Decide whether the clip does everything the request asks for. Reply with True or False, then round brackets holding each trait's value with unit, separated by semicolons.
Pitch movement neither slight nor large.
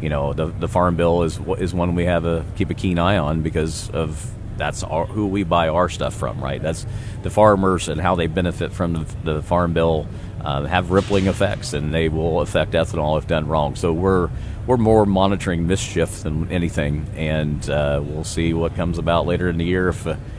True (3.1 semitones)